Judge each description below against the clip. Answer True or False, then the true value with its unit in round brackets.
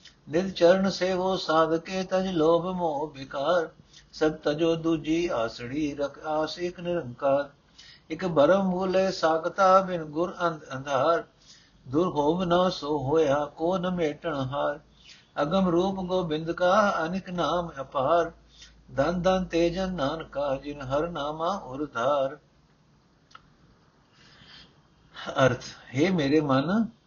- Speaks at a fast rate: False (105 wpm)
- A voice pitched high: False (165 Hz)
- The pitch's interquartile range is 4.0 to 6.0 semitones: False (3.4 semitones)